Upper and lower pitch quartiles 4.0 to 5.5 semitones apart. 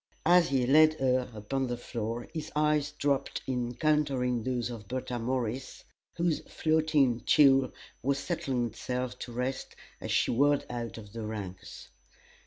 No: average, 3.3 semitones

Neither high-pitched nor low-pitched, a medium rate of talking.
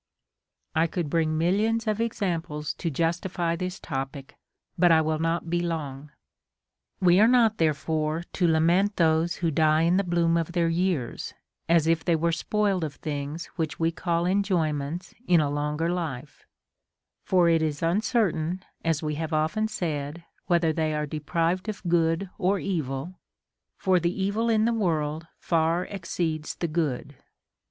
Yes: medium, 165 Hz; average, 160 wpm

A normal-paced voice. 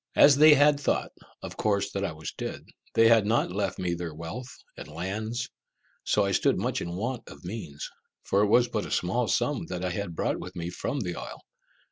No: fast, 220 wpm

